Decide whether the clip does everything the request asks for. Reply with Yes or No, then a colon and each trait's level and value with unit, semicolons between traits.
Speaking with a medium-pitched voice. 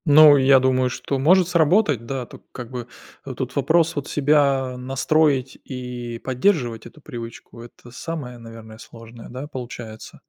No: low, 130 Hz